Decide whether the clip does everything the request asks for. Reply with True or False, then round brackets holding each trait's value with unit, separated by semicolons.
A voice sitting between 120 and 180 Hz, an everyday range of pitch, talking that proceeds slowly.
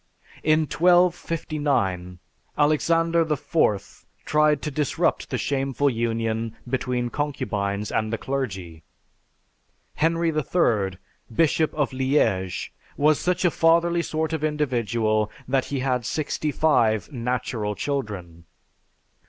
False (135 Hz; 5.9 semitones; 105 wpm)